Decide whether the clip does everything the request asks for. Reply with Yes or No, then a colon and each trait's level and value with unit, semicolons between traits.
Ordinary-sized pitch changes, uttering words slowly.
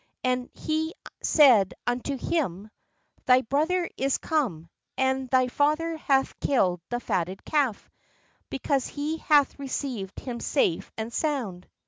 Yes: average, 4.1 semitones; slow, 125 wpm